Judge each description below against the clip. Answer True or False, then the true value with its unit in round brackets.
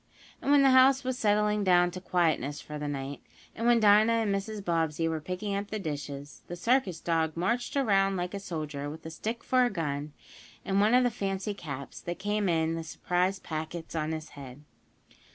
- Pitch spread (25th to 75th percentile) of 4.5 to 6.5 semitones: True (5.0 semitones)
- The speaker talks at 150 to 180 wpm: False (205 wpm)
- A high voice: False (180 Hz)